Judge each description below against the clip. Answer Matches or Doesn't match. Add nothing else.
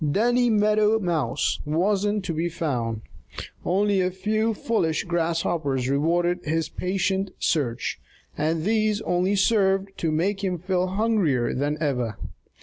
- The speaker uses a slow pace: Matches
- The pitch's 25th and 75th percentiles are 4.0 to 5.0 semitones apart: Matches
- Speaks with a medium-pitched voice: Matches